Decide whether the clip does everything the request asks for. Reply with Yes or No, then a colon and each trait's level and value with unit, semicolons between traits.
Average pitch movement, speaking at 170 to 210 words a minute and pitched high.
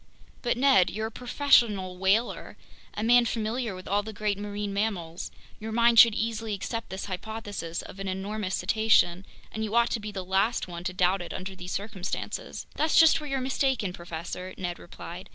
Yes: average, 3.5 semitones; average, 185 wpm; high, 205 Hz